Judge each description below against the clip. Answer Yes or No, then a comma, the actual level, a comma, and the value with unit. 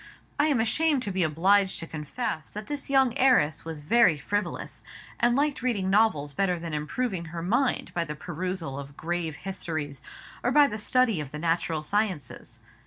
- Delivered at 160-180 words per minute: Yes, average, 175 wpm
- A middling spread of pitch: No, wide, 7.2 semitones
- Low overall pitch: No, medium, 185 Hz